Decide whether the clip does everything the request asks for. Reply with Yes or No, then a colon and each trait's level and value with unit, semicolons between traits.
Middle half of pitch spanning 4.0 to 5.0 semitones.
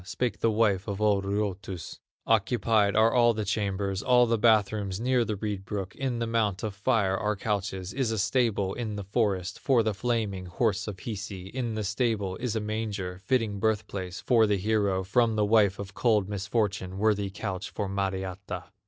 No: narrow, 2.5 semitones